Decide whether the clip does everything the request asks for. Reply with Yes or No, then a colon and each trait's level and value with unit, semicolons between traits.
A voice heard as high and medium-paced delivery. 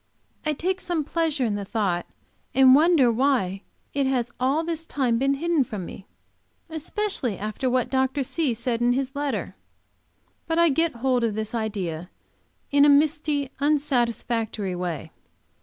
Yes: very high, 265 Hz; average, 155 wpm